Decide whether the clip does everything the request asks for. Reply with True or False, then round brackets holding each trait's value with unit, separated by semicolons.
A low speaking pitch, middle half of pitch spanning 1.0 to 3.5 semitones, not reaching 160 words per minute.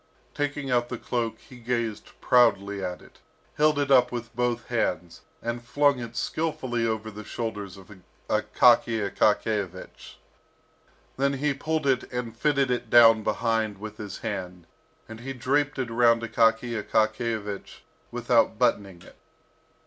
True (115 Hz; 2.7 semitones; 140 wpm)